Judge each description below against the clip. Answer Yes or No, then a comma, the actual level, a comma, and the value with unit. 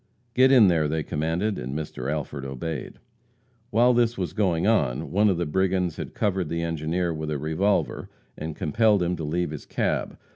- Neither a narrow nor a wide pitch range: Yes, average, 4.2 semitones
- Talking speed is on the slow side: No, average, 185 wpm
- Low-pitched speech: Yes, very low, 85 Hz